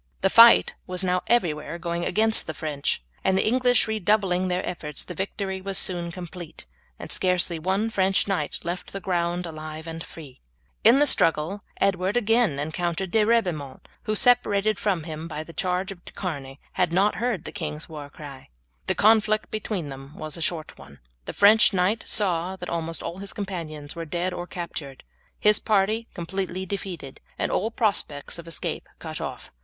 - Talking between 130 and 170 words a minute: No, average, 180 wpm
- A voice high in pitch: No, medium, 180 Hz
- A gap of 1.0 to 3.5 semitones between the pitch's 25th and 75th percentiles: No, average, 3.9 semitones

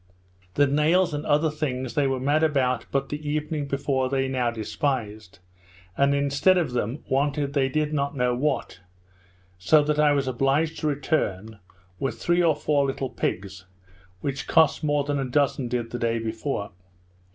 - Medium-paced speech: Yes, average, 170 wpm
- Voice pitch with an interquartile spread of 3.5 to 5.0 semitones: No, average, 3.0 semitones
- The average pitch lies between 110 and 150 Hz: Yes, medium, 140 Hz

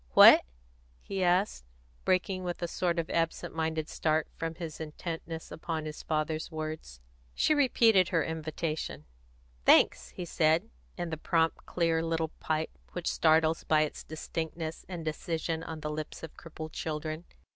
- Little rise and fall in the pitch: Yes, narrow, 1.4 semitones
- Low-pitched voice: No, medium, 160 Hz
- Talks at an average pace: Yes, average, 150 wpm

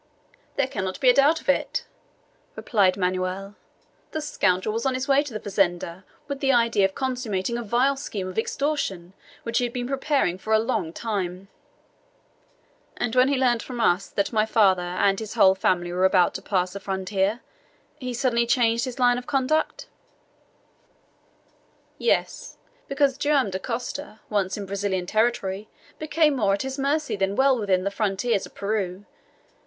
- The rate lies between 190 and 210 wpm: No, average, 170 wpm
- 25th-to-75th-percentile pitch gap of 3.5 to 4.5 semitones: No, average, 5.2 semitones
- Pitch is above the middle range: Yes, high, 220 Hz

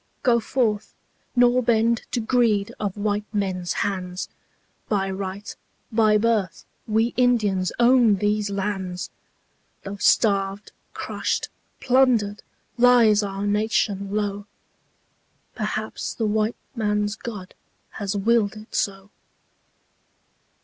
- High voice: Yes, high, 210 Hz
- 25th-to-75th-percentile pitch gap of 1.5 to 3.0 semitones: Yes, narrow, 2.4 semitones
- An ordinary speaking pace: No, slow, 105 wpm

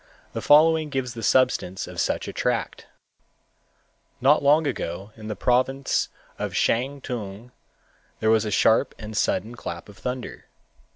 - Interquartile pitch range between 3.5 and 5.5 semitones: Yes, average, 4.0 semitones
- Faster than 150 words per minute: No, average, 140 wpm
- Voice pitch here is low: Yes, low, 120 Hz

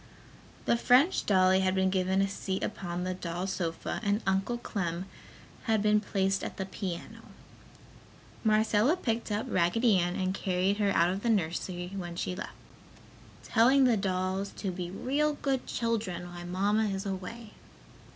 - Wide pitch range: No, average, 3.1 semitones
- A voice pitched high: Yes, high, 195 Hz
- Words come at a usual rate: Yes, average, 160 wpm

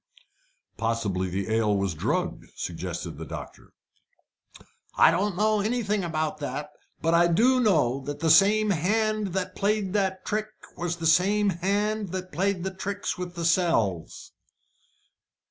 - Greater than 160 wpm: No, average, 145 wpm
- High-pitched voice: No, medium, 180 Hz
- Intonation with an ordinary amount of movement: Yes, average, 5.0 semitones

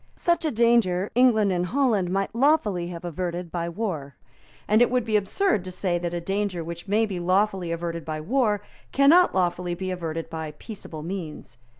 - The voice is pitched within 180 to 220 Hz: Yes, medium, 185 Hz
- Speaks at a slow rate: No, average, 185 wpm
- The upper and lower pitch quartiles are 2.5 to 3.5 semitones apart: No, average, 4.2 semitones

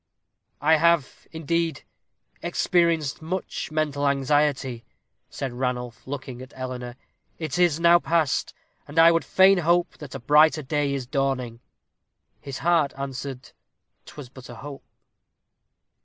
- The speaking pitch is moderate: Yes, medium, 145 Hz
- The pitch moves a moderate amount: Yes, average, 3.9 semitones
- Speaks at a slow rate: Yes, slow, 125 wpm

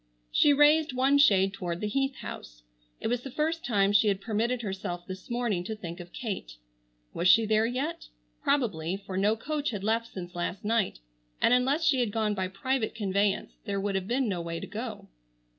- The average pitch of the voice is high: Yes, high, 215 Hz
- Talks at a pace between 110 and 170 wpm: No, average, 200 wpm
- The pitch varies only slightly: No, average, 4.7 semitones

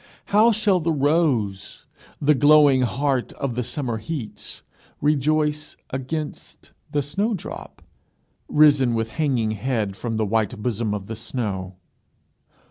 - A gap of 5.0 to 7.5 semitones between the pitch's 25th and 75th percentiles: Yes, average, 5.3 semitones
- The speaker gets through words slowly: Yes, slow, 125 wpm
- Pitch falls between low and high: No, low, 130 Hz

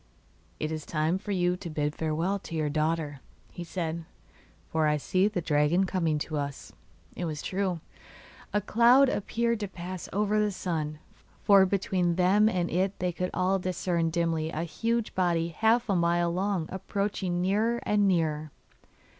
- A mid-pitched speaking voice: Yes, medium, 180 Hz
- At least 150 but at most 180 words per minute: Yes, average, 165 wpm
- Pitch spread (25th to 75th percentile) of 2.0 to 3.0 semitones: No, average, 3.5 semitones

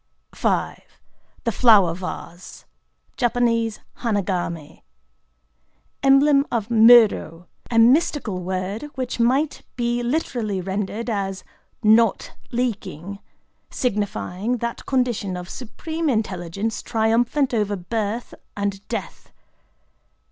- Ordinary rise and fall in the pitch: Yes, average, 4.0 semitones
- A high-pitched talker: Yes, high, 220 Hz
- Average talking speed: No, slow, 85 wpm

